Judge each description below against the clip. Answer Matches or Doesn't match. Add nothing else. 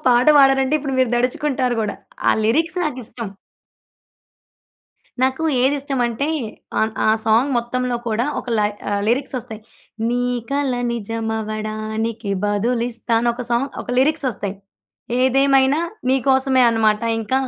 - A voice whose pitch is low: Doesn't match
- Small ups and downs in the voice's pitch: Doesn't match